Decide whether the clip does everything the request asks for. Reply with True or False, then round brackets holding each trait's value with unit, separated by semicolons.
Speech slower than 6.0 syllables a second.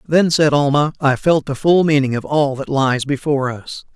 True (4.9 syllables/s)